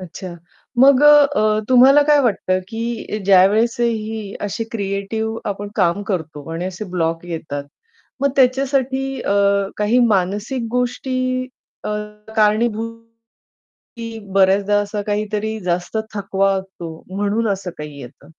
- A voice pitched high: Yes, high, 210 Hz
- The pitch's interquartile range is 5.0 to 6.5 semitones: No, average, 3.5 semitones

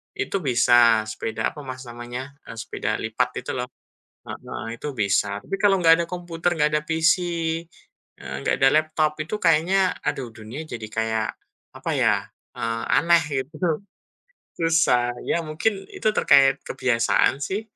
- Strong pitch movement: Yes, wide, 6.0 semitones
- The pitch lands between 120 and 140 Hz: Yes, low, 135 Hz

